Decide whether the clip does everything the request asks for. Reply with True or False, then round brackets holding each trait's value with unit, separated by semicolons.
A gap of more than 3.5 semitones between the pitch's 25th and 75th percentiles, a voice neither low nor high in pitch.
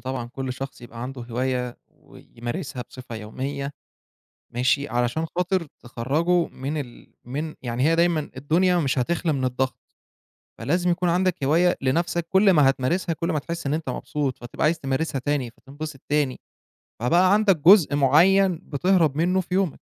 True (4.9 semitones; 145 Hz)